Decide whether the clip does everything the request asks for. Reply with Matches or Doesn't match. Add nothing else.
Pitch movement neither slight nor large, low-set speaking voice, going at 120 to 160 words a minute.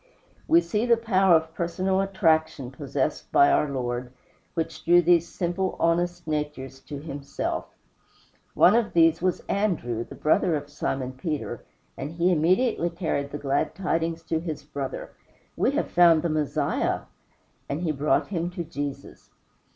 Doesn't match